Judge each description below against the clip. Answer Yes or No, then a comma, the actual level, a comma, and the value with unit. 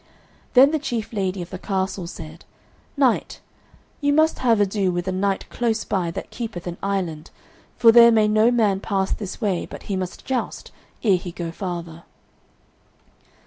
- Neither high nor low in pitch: No, high, 195 Hz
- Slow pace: No, average, 170 wpm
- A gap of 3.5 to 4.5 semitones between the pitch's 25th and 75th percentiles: Yes, average, 4.1 semitones